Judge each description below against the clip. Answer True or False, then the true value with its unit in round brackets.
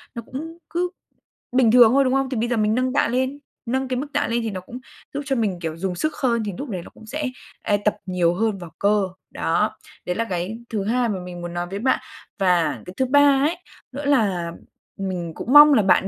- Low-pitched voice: False (225 Hz)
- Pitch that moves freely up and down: True (5.8 semitones)